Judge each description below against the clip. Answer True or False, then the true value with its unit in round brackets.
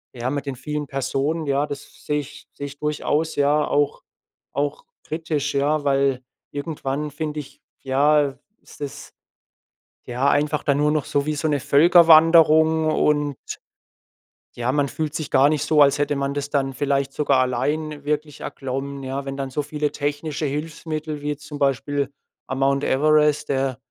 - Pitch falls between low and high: True (145 Hz)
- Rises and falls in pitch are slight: True (1.6 semitones)